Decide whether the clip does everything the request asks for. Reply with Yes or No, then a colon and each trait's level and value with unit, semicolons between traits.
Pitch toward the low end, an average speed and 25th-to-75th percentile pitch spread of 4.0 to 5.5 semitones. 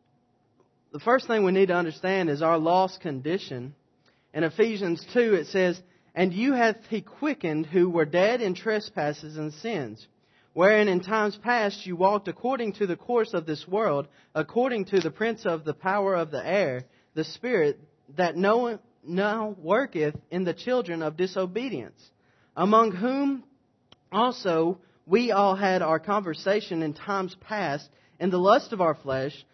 No: medium, 185 Hz; average, 160 wpm; average, 5.2 semitones